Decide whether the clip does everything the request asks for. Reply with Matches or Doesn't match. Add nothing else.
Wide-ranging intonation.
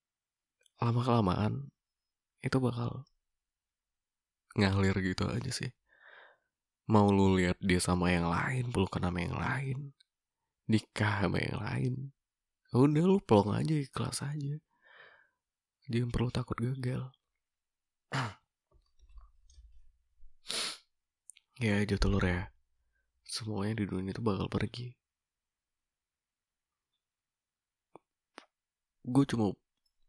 Matches